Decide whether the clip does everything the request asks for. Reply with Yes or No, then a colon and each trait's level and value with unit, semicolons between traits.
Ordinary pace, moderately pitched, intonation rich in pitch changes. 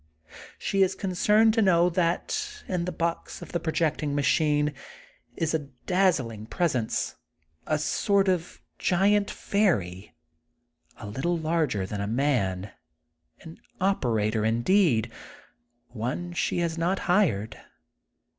No: slow, 115 wpm; medium, 165 Hz; wide, 7.8 semitones